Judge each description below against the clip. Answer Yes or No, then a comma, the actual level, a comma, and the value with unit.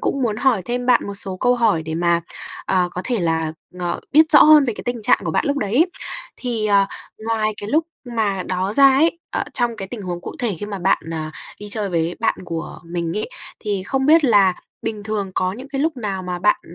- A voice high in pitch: Yes, high, 210 Hz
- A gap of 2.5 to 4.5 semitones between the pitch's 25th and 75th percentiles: No, average, 5.2 semitones